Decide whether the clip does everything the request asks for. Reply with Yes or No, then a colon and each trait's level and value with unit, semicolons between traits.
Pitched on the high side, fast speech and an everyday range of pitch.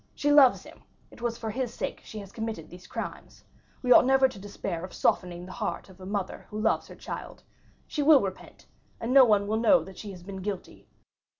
Yes: high, 210 Hz; fast, 220 wpm; average, 4.5 semitones